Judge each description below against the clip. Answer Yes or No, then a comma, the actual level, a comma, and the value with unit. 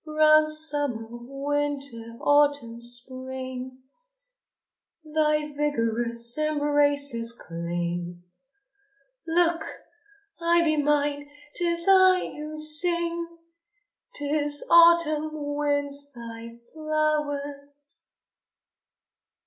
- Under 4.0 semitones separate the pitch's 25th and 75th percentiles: Yes, average, 3.2 semitones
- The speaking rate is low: Yes, slow, 65 wpm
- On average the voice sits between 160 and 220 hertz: No, very high, 290 Hz